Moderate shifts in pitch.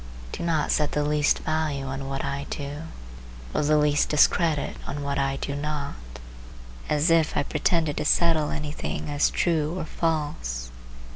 No: narrow, 1.8 semitones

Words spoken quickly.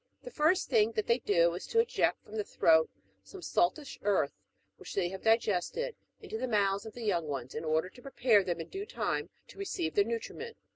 Yes: fast, 220 wpm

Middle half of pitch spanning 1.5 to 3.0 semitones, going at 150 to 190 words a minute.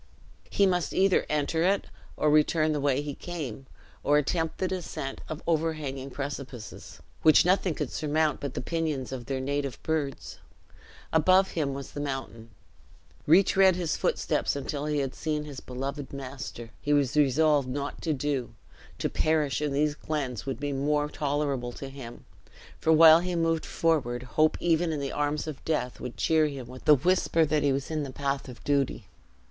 Yes: average, 2.7 semitones; average, 175 wpm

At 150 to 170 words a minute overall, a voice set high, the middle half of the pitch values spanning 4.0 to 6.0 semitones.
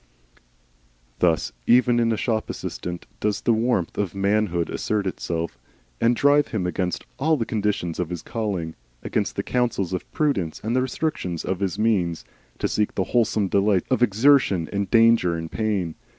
No: average, 165 wpm; low, 105 Hz; average, 4.7 semitones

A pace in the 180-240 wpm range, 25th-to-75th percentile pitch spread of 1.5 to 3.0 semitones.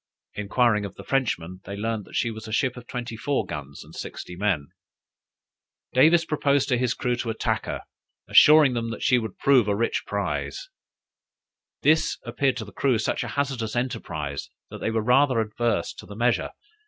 No: average, 185 wpm; average, 3.7 semitones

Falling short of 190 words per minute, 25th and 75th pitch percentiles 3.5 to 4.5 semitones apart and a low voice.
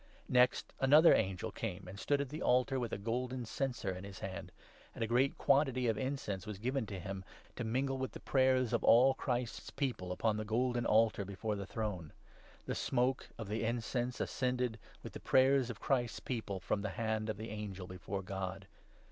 No: average, 200 wpm; average, 4.1 semitones; low, 115 Hz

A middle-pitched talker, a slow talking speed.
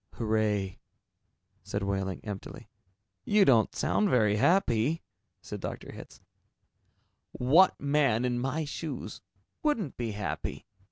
No: low, 120 Hz; slow, 110 wpm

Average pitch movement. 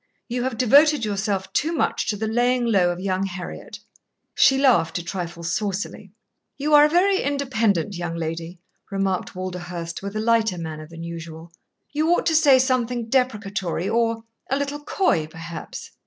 No: wide, 6.6 semitones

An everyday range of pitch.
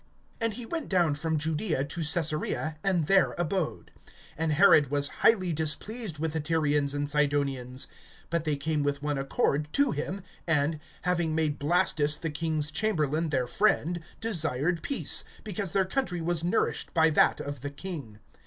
Yes: average, 3.4 semitones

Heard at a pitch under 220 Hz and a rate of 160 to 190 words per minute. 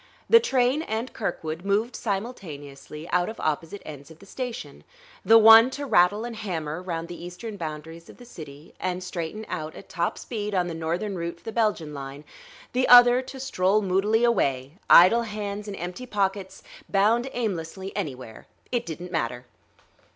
Yes: high, 190 Hz; average, 170 wpm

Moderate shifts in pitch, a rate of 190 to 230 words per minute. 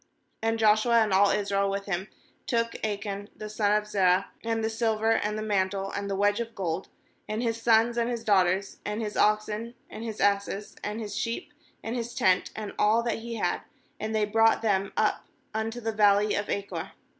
No: narrow, 2.0 semitones; average, 200 wpm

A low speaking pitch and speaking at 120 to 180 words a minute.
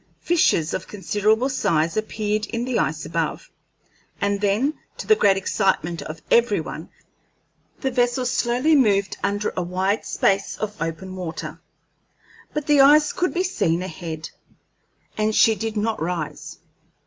No: high, 205 Hz; average, 145 wpm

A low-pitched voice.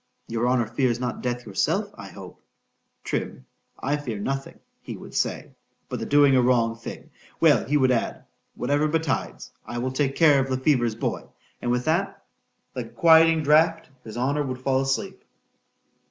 Yes: low, 130 Hz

